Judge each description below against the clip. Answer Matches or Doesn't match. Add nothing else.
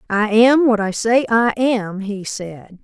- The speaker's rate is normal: Matches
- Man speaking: Doesn't match